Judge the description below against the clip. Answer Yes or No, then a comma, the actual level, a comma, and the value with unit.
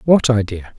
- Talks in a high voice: No, low, 115 Hz